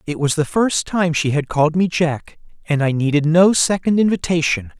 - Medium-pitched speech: Yes, medium, 165 Hz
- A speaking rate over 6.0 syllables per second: No, 5.0 syllables/s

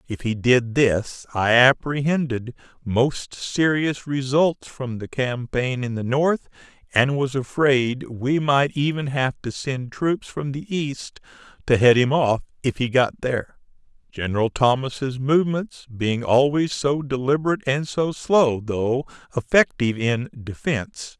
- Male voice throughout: Yes, male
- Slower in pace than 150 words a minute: Yes, average, 140 wpm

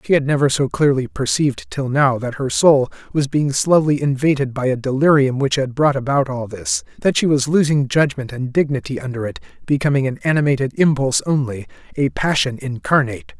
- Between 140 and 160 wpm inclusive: No, average, 185 wpm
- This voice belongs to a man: Yes, male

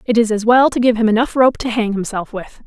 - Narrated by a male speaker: No, female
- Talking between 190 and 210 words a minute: No, fast, 290 wpm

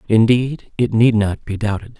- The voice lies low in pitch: Yes, low, 110 Hz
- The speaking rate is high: No, average, 180 wpm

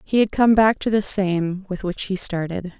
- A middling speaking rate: No, fast, 235 wpm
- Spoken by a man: No, female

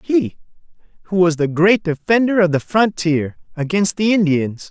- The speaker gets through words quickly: No, average, 155 wpm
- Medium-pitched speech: Yes, medium, 170 Hz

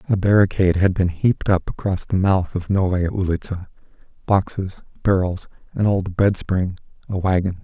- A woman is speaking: No, male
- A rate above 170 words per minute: No, average, 150 wpm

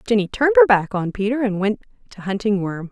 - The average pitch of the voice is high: Yes, high, 205 Hz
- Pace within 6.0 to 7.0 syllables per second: Yes, 6.2 syllables/s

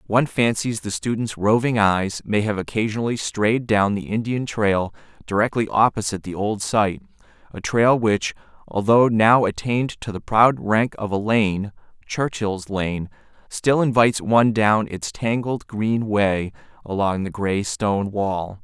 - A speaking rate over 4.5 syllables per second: No, 4.4 syllables/s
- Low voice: Yes, low, 105 Hz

